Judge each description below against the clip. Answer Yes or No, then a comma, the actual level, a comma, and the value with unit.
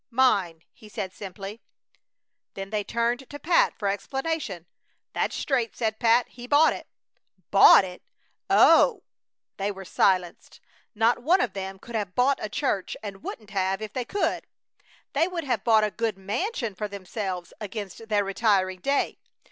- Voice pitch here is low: No, high, 215 Hz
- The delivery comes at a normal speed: Yes, average, 160 wpm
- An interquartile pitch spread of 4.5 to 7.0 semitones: No, average, 4.1 semitones